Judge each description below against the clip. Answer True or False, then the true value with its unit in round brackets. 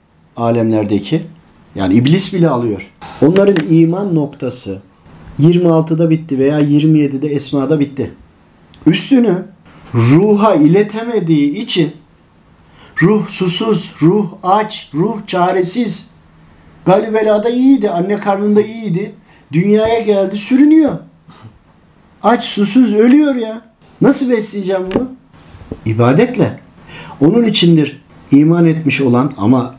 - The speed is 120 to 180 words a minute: False (95 wpm)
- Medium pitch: True (175 Hz)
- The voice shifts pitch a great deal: True (6.5 semitones)